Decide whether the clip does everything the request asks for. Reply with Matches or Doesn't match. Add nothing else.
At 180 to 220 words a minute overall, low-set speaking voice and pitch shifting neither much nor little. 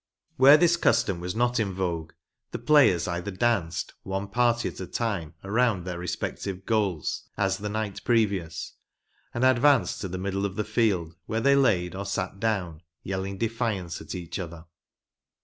Doesn't match